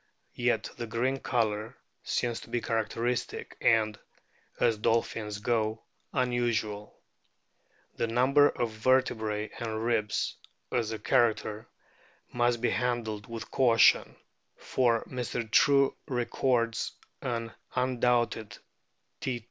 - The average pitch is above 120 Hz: No, low, 115 Hz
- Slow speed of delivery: Yes, slow, 110 wpm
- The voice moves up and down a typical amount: No, narrow, 2.0 semitones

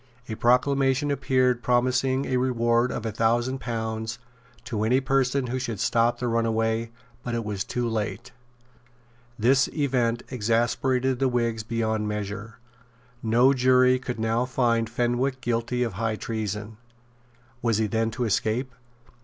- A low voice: Yes, low, 120 Hz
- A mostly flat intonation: Yes, narrow, 2.3 semitones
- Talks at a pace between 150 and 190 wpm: No, average, 140 wpm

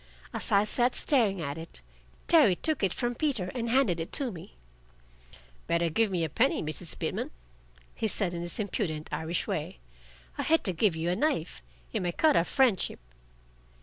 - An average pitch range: No, wide, 6.4 semitones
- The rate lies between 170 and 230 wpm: Yes, average, 180 wpm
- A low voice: No, high, 190 Hz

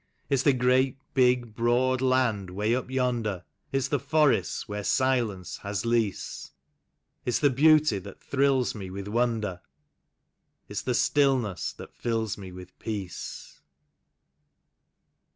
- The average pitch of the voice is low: Yes, low, 120 Hz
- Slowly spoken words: Yes, slow, 125 wpm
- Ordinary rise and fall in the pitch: Yes, average, 4.2 semitones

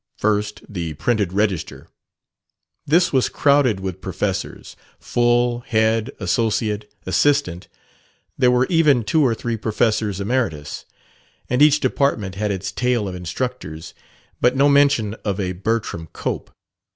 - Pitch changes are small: No, average, 4.6 semitones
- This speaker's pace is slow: Yes, slow, 125 wpm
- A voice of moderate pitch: No, low, 110 Hz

